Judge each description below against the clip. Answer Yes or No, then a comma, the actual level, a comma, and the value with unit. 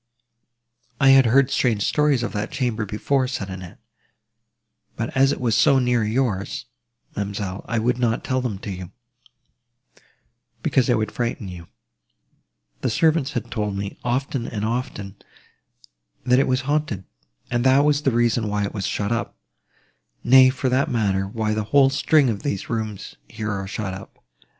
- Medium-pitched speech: No, low, 115 Hz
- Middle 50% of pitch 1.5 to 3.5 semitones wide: No, average, 4.1 semitones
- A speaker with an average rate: Yes, average, 165 wpm